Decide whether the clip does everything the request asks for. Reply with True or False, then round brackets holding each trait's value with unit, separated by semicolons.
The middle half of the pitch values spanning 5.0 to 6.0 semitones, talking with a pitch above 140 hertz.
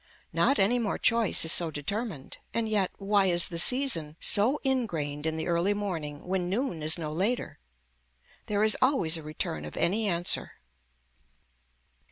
True (5.4 semitones; 185 Hz)